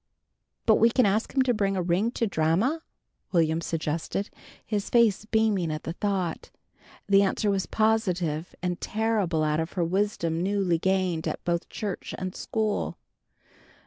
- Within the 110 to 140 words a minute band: No, average, 155 wpm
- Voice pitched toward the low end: No, high, 190 Hz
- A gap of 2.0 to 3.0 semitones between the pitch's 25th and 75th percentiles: No, average, 4.1 semitones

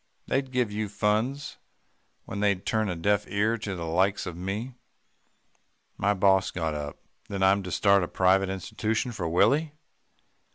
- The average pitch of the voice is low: Yes, low, 100 Hz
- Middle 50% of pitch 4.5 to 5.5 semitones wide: No, average, 2.8 semitones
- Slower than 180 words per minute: Yes, average, 160 wpm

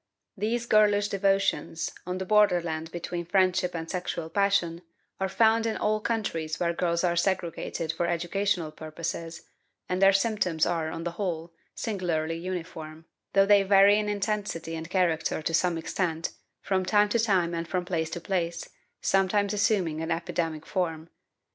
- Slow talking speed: No, average, 155 wpm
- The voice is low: No, medium, 180 Hz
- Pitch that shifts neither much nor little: Yes, average, 3.2 semitones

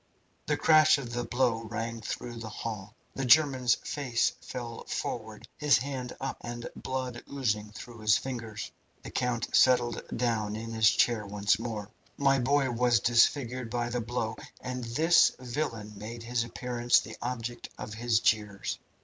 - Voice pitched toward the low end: Yes, low, 120 Hz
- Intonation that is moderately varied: No, narrow, 2.1 semitones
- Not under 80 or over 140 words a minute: No, average, 160 wpm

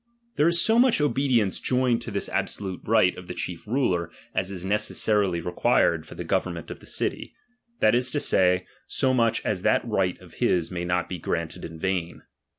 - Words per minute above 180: Yes, average, 200 wpm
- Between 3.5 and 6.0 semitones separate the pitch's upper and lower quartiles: Yes, wide, 5.6 semitones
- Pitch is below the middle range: Yes, very low, 95 Hz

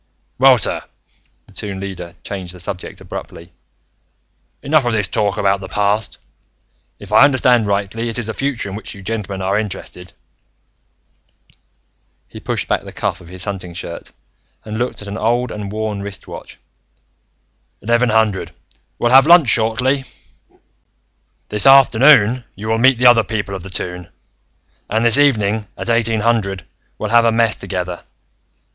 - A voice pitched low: Yes, low, 110 Hz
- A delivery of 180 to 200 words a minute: No, average, 160 wpm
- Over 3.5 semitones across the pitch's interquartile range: No, average, 3.2 semitones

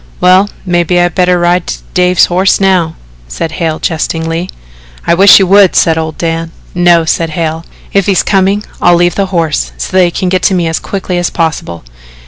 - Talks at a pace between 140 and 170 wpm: No, average, 190 wpm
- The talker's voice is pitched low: No, medium, 175 Hz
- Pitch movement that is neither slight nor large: No, narrow, 2.2 semitones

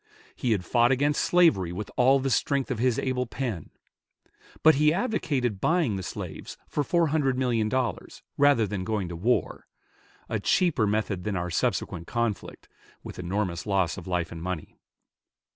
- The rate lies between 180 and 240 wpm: No, average, 165 wpm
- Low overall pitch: Yes, low, 115 Hz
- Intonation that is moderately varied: No, wide, 6.4 semitones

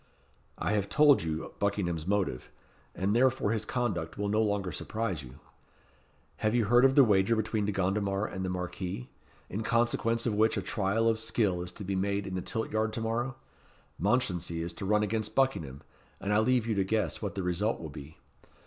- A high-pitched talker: No, low, 105 Hz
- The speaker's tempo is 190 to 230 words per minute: Yes, average, 200 wpm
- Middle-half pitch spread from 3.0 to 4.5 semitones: Yes, average, 3.3 semitones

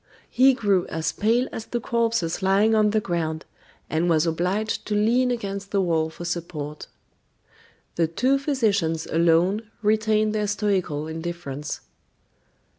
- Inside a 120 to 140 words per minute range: Yes, slow, 135 wpm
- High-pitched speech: Yes, high, 195 Hz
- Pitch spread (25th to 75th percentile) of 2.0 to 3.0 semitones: No, average, 4.9 semitones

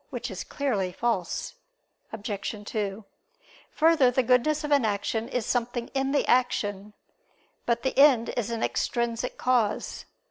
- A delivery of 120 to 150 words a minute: Yes, average, 140 wpm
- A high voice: Yes, high, 235 Hz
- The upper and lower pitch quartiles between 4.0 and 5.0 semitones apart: No, average, 3.4 semitones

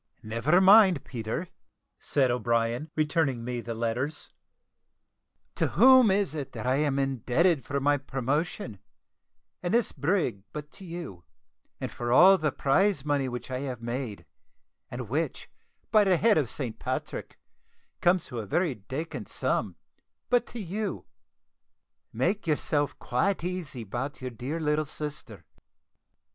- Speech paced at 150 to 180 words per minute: No, average, 140 wpm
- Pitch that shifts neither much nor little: No, wide, 6.1 semitones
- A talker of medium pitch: Yes, medium, 145 Hz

